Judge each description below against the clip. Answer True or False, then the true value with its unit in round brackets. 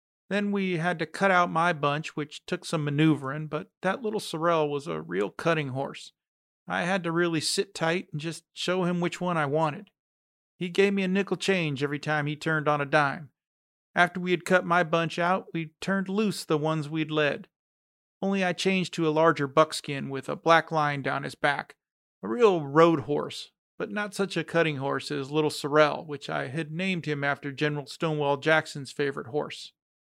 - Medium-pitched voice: True (160 Hz)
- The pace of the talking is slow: False (200 wpm)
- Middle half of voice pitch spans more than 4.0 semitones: False (3.2 semitones)